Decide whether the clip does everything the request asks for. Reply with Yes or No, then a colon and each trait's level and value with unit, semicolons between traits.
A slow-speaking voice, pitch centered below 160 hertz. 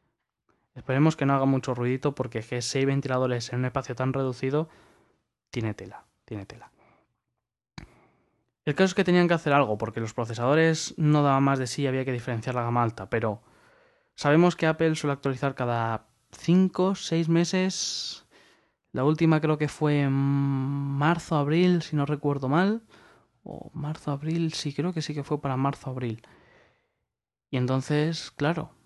No: average, 160 wpm; medium, 140 Hz